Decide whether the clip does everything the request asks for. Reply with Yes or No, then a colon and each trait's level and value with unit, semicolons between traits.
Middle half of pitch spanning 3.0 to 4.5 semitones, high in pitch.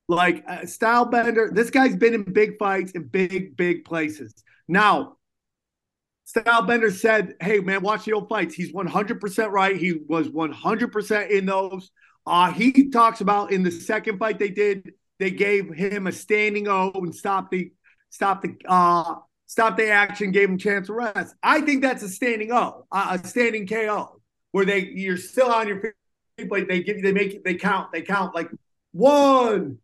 Yes: average, 3.3 semitones; high, 200 Hz